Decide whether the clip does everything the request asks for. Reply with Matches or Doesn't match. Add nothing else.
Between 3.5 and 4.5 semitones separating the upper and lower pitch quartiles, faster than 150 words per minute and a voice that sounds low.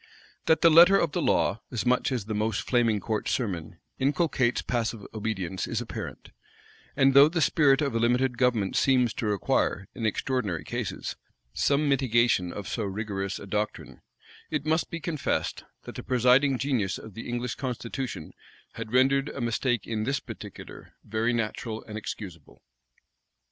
Matches